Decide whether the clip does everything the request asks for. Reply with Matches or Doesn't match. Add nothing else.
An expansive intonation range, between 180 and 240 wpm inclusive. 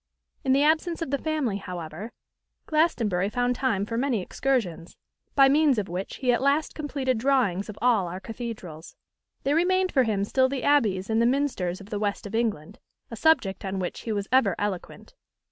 Matches